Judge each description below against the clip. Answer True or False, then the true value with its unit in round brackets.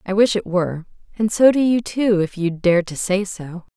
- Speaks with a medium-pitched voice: False (195 Hz)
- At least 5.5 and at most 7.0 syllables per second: False (4.9 syllables/s)